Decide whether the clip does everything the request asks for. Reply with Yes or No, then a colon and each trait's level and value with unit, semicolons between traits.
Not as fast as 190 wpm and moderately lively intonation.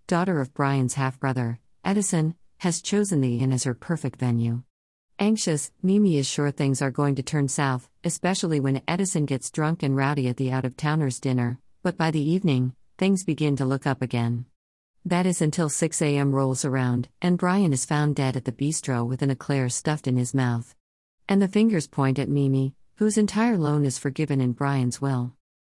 No: average, 195 wpm; average, 4.1 semitones